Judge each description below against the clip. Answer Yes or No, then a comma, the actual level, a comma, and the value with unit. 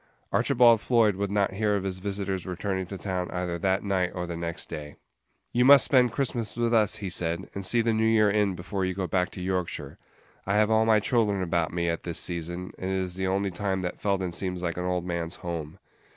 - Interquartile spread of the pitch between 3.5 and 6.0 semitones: No, average, 2.8 semitones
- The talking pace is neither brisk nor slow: No, fast, 230 wpm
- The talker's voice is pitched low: Yes, very low, 95 Hz